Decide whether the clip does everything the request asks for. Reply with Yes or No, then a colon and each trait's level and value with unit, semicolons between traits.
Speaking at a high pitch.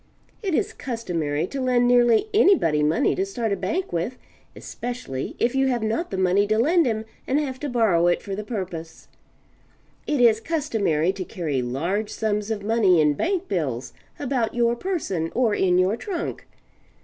Yes: high, 220 Hz